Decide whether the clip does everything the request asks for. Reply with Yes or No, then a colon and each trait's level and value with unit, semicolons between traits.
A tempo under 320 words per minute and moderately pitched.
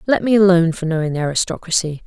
Yes: fast, 205 wpm; medium, 175 Hz